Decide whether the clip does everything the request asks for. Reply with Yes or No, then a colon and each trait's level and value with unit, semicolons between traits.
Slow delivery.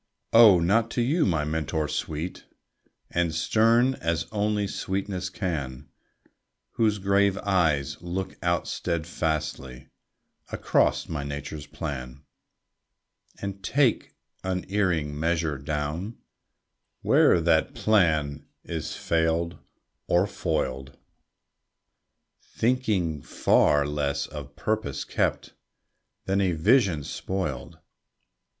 Yes: slow, 95 wpm